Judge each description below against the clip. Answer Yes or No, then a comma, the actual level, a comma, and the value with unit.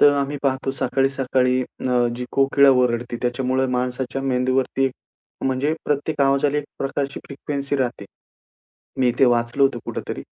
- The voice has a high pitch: No, low, 135 Hz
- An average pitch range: No, narrow, 1.6 semitones